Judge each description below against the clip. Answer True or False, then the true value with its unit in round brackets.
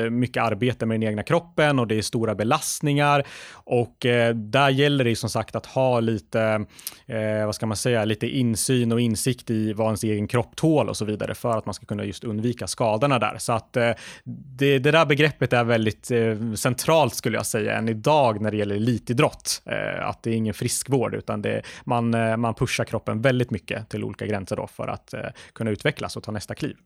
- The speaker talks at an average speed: False (200 wpm)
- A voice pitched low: True (115 Hz)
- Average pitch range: True (3.0 semitones)